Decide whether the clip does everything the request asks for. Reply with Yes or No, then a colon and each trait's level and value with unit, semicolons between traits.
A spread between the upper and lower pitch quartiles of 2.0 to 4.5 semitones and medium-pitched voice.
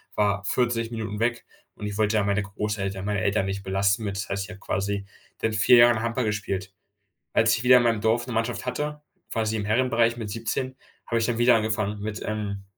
No: narrow, 2.5 semitones; low, 110 Hz